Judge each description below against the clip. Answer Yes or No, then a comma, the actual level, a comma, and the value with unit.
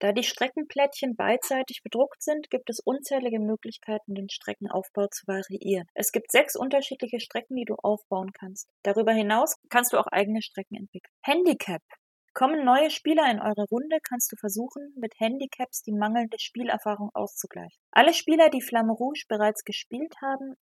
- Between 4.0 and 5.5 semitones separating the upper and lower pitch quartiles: Yes, average, 4.3 semitones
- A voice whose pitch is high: Yes, high, 235 Hz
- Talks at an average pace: Yes, average, 160 wpm